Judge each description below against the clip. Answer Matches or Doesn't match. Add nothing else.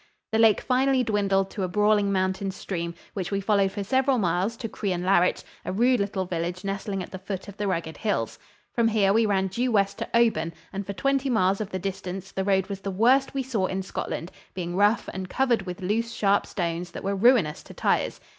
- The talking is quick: Matches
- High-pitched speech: Matches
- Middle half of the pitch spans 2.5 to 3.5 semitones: Matches